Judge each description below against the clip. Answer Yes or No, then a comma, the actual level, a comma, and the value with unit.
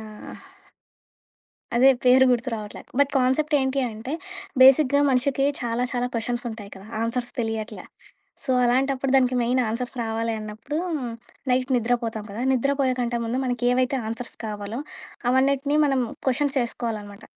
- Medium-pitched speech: No, very high, 250 Hz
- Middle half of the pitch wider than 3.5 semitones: No, narrow, 2.6 semitones